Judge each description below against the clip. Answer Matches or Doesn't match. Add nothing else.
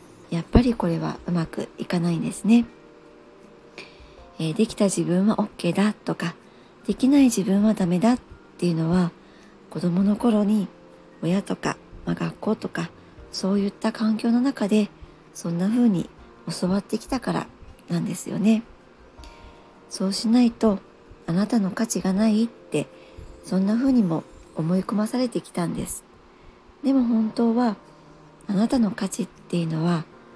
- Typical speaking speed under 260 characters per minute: Doesn't match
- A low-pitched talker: Doesn't match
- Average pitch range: Matches